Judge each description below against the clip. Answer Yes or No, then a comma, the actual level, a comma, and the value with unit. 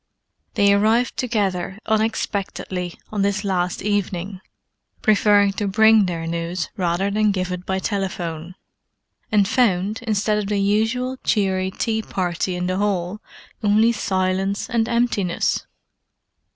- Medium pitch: No, high, 200 Hz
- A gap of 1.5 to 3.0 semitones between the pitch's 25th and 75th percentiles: Yes, average, 2.7 semitones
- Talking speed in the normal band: No, slow, 125 wpm